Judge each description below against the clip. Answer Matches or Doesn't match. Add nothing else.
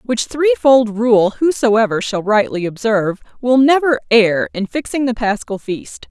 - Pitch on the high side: Matches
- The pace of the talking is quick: Doesn't match